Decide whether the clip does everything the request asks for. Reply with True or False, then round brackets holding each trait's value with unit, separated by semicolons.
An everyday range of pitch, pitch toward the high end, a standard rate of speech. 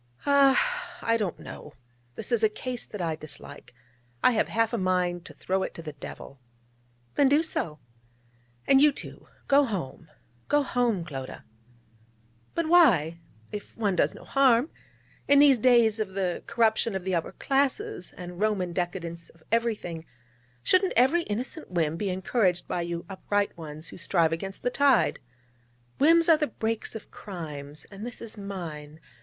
False (6.7 semitones; 205 Hz; 165 wpm)